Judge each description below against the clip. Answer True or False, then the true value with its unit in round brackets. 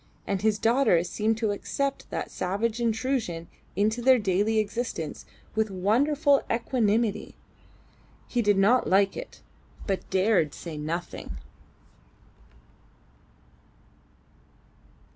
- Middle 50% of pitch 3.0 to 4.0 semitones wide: True (3.7 semitones)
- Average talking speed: False (100 wpm)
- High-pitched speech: True (215 Hz)